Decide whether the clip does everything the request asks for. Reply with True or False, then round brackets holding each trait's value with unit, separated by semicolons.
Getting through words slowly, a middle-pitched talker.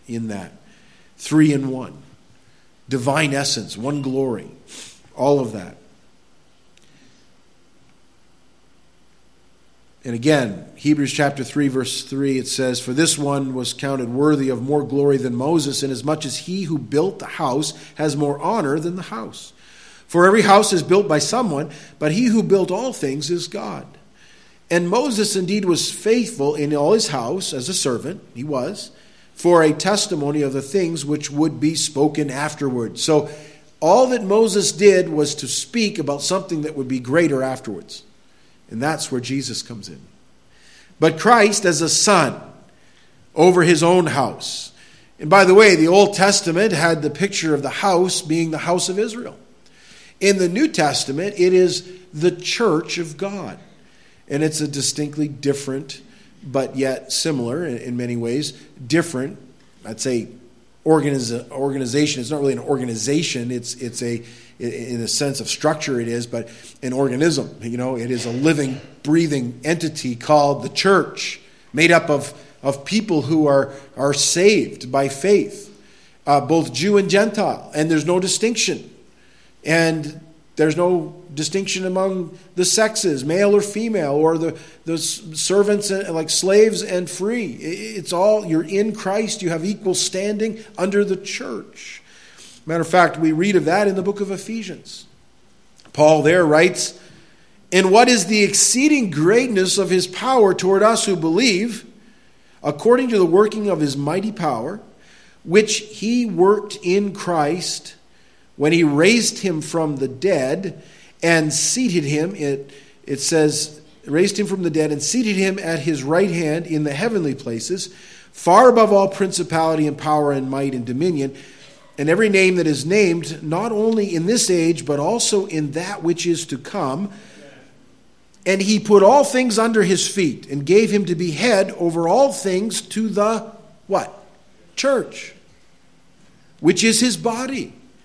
False (155 wpm; 165 Hz)